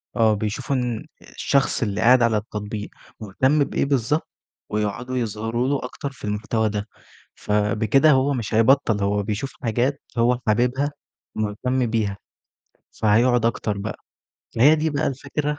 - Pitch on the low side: Yes, low, 115 Hz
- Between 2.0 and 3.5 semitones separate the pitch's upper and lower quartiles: No, average, 3.9 semitones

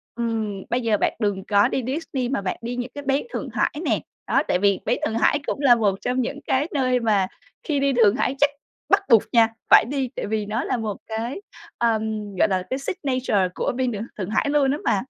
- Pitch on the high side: Yes, high, 235 Hz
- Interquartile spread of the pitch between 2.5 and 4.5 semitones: Yes, average, 4.0 semitones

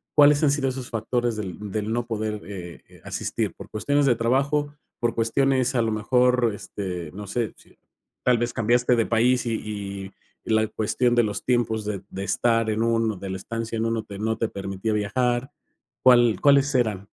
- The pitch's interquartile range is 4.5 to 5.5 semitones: No, average, 2.8 semitones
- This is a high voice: No, low, 115 Hz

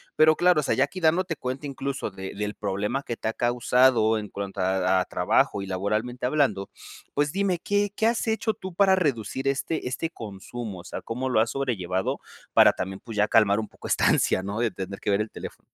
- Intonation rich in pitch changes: Yes, wide, 6.6 semitones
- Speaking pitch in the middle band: No, low, 120 Hz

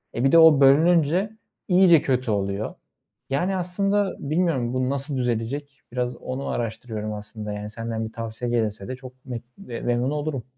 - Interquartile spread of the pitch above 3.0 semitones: Yes, average, 5.0 semitones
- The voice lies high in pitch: No, low, 130 Hz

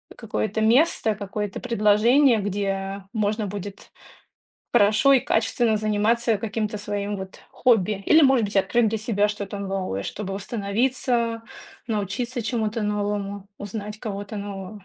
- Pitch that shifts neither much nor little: No, narrow, 2.2 semitones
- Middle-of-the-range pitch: No, high, 210 Hz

